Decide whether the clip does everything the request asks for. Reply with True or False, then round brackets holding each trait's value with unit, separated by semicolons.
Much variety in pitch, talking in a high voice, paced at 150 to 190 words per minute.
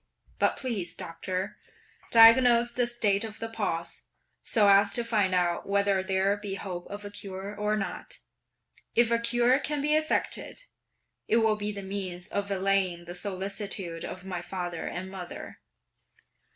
False (3.2 semitones; 200 Hz; 155 wpm)